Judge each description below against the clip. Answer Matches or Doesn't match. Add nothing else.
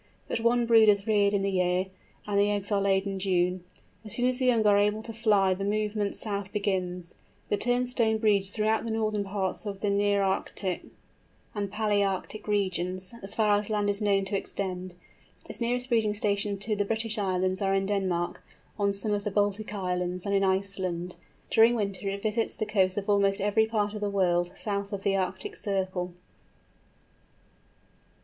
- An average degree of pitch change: Doesn't match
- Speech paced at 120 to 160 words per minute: Doesn't match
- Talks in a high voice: Matches